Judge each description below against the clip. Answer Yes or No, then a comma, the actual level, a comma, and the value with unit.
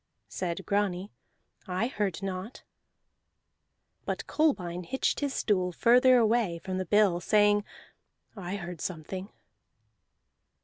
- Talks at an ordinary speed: No, slow, 105 wpm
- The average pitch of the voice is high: Yes, high, 195 Hz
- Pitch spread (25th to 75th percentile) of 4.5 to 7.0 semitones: No, average, 3.2 semitones